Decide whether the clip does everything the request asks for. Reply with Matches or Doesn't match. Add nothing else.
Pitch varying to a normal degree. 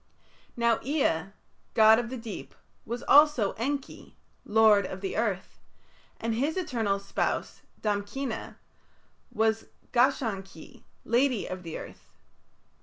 Matches